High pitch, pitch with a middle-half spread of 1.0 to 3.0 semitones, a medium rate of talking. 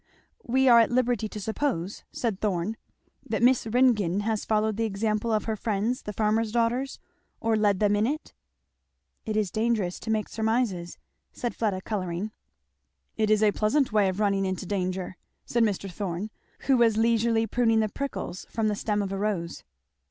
Yes: high, 215 Hz; narrow, 2.4 semitones; average, 180 wpm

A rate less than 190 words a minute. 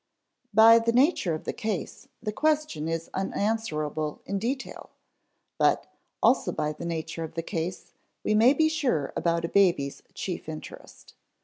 Yes: average, 150 wpm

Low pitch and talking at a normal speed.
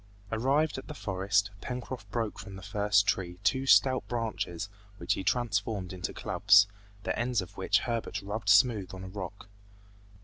Yes: low, 105 Hz; average, 165 wpm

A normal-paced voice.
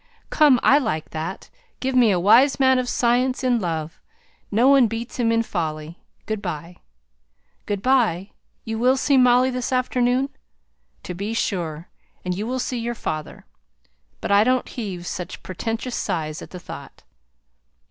Yes: average, 160 wpm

